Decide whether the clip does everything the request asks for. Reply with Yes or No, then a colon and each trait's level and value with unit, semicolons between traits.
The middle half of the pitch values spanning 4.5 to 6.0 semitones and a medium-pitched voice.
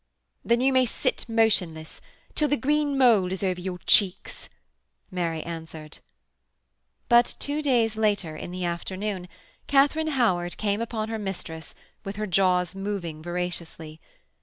No: average, 5.0 semitones; high, 195 Hz